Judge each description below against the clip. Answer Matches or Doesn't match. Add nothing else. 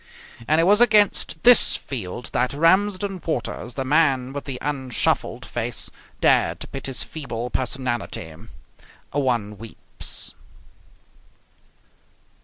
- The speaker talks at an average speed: Doesn't match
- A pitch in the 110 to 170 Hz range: Matches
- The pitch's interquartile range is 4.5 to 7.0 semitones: Matches